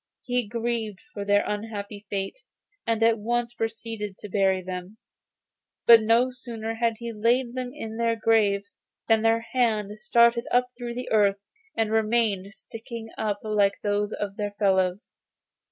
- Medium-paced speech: Yes, average, 155 wpm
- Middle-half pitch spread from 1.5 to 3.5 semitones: Yes, narrow, 2.4 semitones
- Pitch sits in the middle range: No, high, 220 Hz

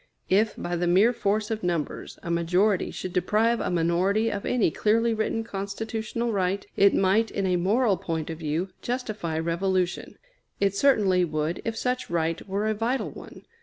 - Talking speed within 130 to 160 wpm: No, average, 170 wpm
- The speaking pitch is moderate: No, high, 195 Hz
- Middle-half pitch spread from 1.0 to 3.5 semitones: No, average, 4.0 semitones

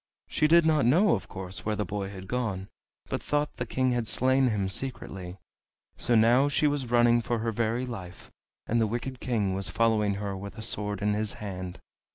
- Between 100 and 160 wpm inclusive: No, fast, 205 wpm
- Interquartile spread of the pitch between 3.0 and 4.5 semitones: Yes, average, 4.0 semitones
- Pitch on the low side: Yes, low, 110 Hz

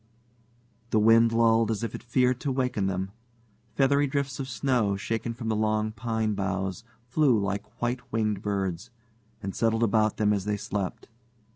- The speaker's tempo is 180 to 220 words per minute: No, average, 165 wpm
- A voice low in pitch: Yes, low, 110 Hz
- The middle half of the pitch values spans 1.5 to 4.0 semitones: Yes, average, 2.9 semitones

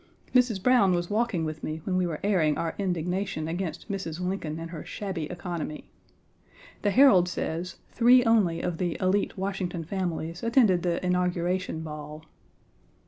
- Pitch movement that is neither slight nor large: Yes, average, 3.1 semitones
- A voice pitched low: No, medium, 180 Hz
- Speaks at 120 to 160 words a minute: Yes, average, 150 wpm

